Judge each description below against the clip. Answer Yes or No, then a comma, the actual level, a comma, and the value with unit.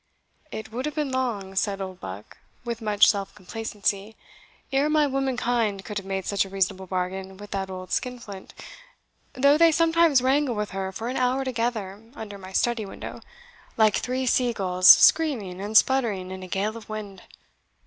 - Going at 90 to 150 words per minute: No, average, 175 wpm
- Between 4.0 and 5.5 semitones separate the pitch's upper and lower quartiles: Yes, average, 4.7 semitones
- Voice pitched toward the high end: Yes, high, 215 Hz